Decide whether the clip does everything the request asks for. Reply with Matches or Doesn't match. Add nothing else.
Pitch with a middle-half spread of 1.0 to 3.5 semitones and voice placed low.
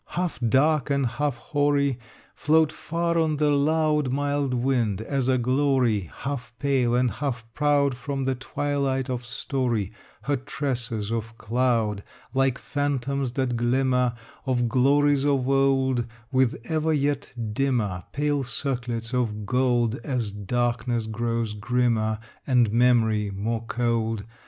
Matches